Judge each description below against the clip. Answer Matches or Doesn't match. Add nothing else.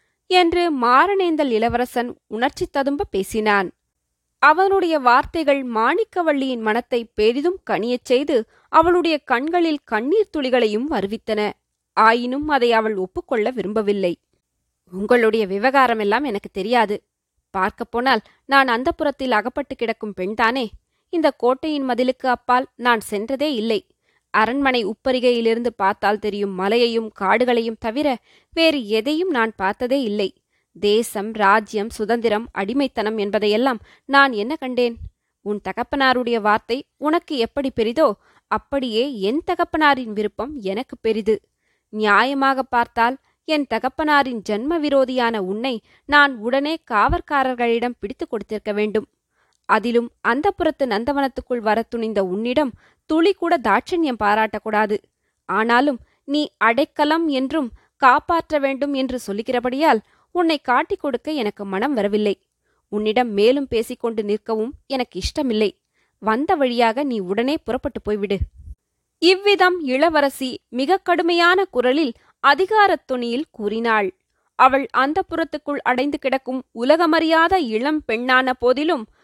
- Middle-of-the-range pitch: Doesn't match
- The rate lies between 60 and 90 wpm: Doesn't match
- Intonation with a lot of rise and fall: Doesn't match